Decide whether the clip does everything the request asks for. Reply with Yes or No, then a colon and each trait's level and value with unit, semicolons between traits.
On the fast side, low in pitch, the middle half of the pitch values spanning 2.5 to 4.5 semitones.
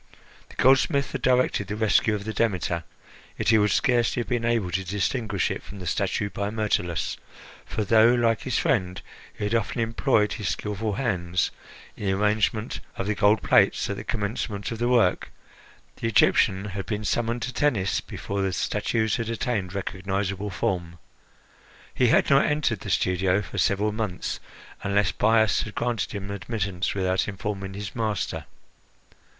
No: average, 165 wpm; low, 105 Hz; average, 2.9 semitones